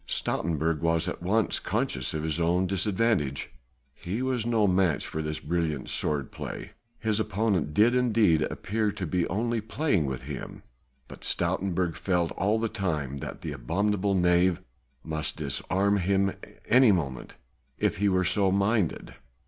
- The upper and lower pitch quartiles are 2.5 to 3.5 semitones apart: No, average, 4.7 semitones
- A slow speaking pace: No, average, 155 wpm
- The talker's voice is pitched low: Yes, very low, 95 Hz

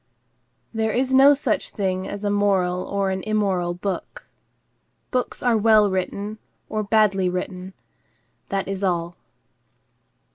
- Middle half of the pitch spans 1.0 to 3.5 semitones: Yes, narrow, 2.6 semitones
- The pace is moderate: No, slow, 130 wpm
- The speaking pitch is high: Yes, high, 200 Hz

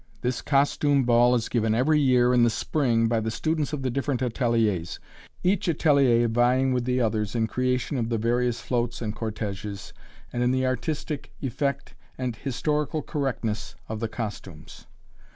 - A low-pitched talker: Yes, low, 125 Hz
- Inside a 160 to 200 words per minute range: Yes, average, 165 wpm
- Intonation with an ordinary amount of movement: Yes, average, 3.0 semitones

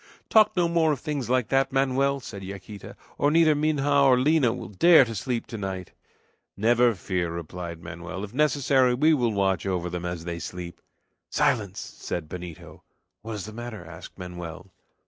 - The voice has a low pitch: Yes, low, 110 Hz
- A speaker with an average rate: Yes, average, 170 wpm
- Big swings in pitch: Yes, wide, 7.3 semitones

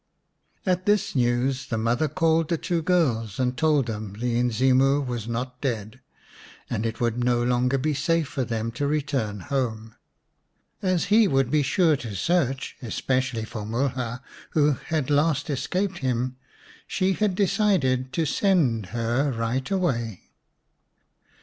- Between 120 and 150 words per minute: Yes, average, 145 wpm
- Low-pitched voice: Yes, low, 130 Hz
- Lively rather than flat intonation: No, average, 4.9 semitones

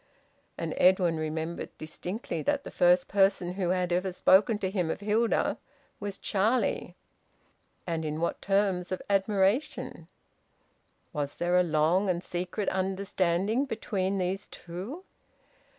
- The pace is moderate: No, slow, 130 wpm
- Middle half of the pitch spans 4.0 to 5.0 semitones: No, narrow, 2.5 semitones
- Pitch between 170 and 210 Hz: Yes, medium, 185 Hz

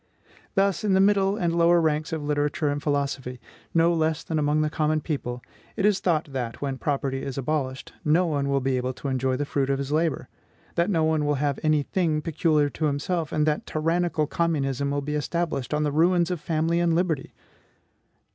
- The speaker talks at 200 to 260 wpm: Yes, fast, 205 wpm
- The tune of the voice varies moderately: Yes, average, 3.0 semitones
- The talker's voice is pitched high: No, medium, 150 Hz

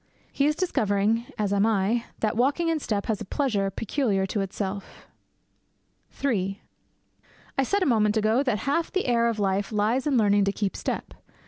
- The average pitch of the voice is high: Yes, high, 220 Hz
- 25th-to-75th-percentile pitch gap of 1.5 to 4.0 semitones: No, average, 4.7 semitones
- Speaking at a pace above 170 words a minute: Yes, average, 180 wpm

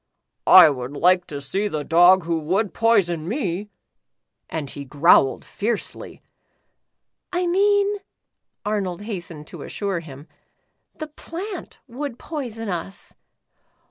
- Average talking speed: No, slow, 125 wpm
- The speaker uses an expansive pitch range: Yes, wide, 6.5 semitones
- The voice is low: No, high, 190 Hz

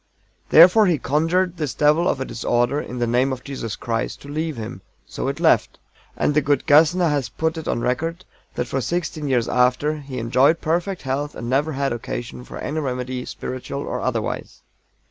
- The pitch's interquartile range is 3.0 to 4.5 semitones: Yes, average, 4.1 semitones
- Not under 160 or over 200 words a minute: Yes, average, 190 wpm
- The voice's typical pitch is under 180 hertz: Yes, medium, 140 Hz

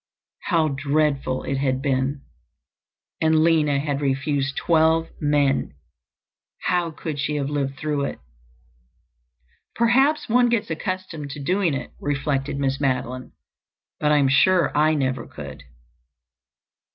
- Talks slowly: Yes, slow, 125 wpm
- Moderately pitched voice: Yes, medium, 145 Hz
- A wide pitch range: No, average, 2.9 semitones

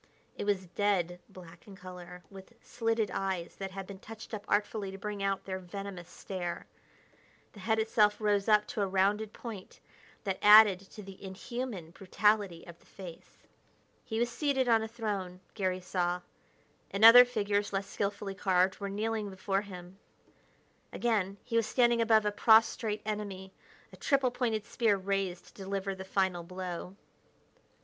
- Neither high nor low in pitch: No, high, 200 Hz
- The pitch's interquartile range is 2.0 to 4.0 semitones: Yes, narrow, 2.6 semitones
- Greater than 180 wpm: No, average, 160 wpm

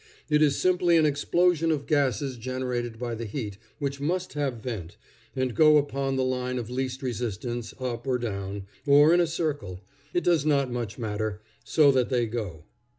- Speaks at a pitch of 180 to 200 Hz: No, low, 130 Hz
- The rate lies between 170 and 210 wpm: Yes, average, 180 wpm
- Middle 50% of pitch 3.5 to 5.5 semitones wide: Yes, average, 3.9 semitones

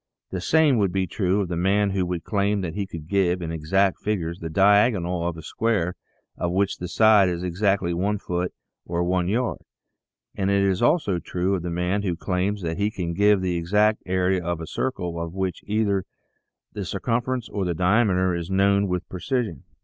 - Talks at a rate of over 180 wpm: Yes, fast, 205 wpm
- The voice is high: No, very low, 95 Hz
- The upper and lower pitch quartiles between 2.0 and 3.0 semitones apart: Yes, average, 2.7 semitones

